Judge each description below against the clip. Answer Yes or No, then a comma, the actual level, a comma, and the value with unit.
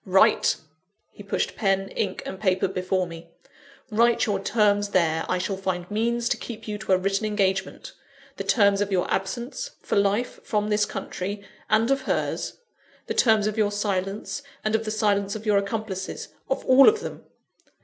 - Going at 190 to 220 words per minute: No, average, 180 wpm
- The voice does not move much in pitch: Yes, narrow, 2.2 semitones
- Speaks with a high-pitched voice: Yes, high, 205 Hz